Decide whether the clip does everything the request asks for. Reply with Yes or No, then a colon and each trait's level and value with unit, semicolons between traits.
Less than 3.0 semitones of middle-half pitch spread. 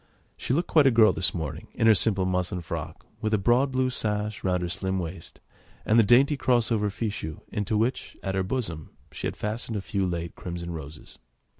No: average, 4.4 semitones